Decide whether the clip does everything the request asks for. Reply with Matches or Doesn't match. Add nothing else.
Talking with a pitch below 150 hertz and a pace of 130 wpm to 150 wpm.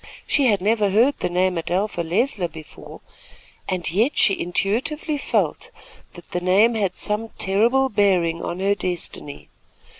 Doesn't match